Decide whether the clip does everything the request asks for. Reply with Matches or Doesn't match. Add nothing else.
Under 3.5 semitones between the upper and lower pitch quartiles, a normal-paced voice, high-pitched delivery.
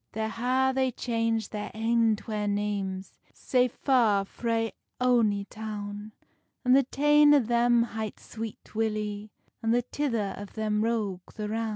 Matches